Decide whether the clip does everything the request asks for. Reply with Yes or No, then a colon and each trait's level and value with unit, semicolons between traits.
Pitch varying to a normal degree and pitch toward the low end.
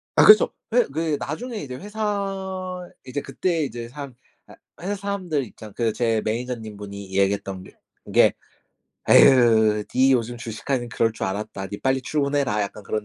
No: wide, 7.4 semitones; low, 125 Hz